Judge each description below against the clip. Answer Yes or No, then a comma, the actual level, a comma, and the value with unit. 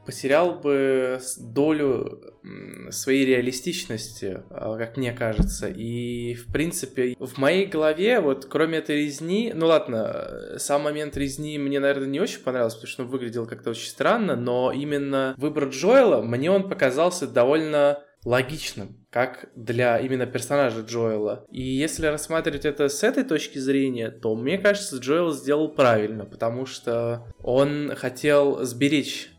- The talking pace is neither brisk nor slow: Yes, average, 140 wpm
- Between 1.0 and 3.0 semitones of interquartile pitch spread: No, average, 3.5 semitones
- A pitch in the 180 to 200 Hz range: No, low, 135 Hz